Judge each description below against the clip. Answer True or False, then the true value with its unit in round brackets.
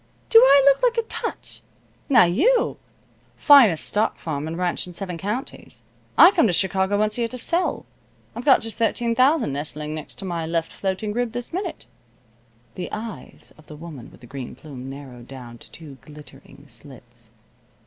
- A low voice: False (185 Hz)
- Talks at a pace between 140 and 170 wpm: False (185 wpm)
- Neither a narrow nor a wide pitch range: False (8.7 semitones)